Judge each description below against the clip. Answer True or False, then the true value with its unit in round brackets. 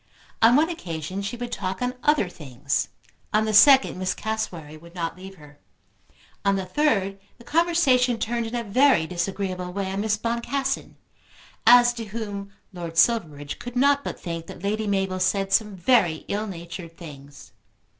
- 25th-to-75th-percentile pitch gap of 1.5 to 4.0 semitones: False (5.3 semitones)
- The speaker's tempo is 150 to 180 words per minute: True (165 wpm)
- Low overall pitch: False (200 Hz)